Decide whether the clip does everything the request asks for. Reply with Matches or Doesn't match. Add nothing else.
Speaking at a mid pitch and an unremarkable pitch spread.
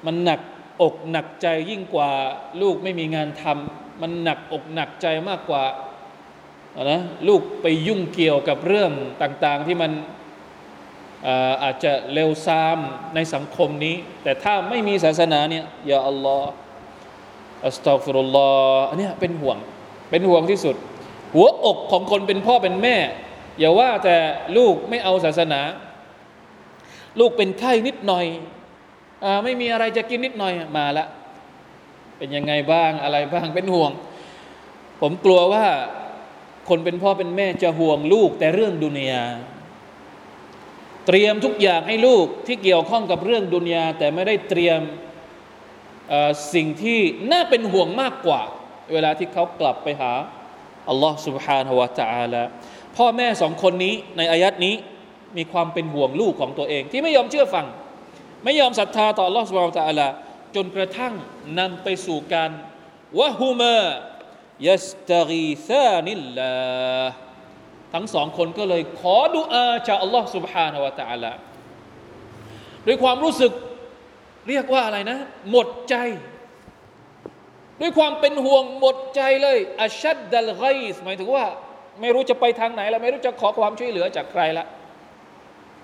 Doesn't match